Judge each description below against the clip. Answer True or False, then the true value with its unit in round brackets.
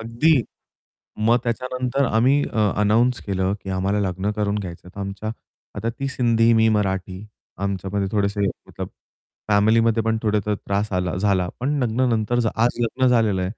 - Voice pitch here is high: False (105 Hz)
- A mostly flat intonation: False (3.0 semitones)